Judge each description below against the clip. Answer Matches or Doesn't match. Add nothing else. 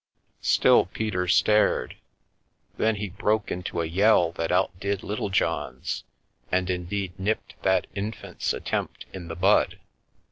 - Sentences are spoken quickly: Doesn't match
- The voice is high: Doesn't match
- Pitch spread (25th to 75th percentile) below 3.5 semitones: Matches